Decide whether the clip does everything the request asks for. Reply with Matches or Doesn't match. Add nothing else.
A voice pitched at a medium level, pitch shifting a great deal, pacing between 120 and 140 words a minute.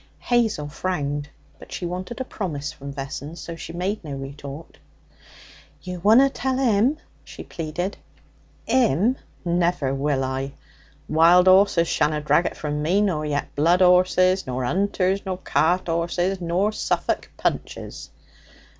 Doesn't match